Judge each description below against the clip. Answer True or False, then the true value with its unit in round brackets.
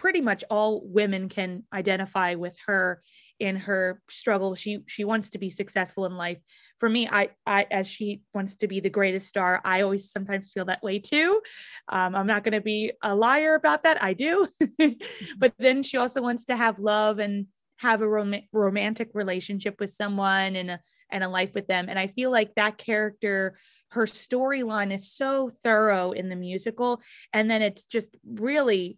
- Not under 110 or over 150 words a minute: False (190 wpm)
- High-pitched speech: True (205 Hz)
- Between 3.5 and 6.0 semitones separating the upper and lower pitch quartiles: False (2.8 semitones)